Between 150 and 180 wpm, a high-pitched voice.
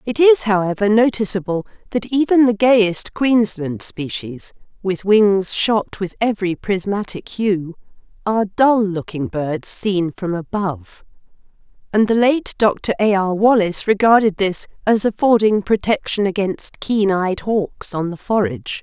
No: slow, 135 wpm; high, 200 Hz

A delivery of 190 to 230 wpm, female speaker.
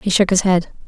No: fast, 275 wpm; female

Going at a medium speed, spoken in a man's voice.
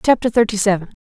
No: average, 175 wpm; female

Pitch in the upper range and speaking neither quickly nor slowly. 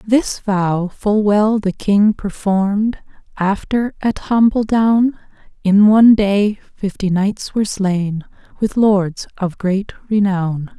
No: high, 205 Hz; slow, 120 wpm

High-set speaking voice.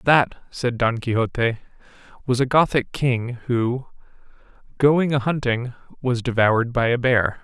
No: low, 125 Hz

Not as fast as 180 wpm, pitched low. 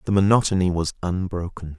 Yes: slow, 135 wpm; very low, 90 Hz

